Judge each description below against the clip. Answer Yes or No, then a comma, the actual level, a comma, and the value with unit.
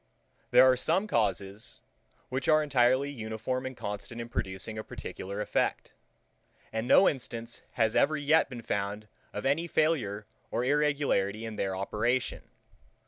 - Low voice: Yes, low, 120 Hz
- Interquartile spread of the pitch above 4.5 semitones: Yes, average, 4.9 semitones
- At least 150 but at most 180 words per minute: No, average, 140 wpm